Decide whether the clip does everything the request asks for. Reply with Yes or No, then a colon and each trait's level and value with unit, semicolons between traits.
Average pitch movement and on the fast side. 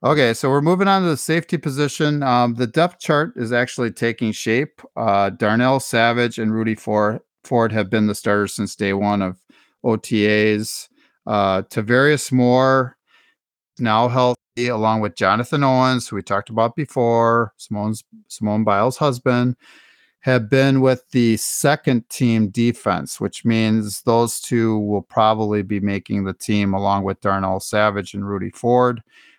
No: average, 3.4 semitones; average, 150 wpm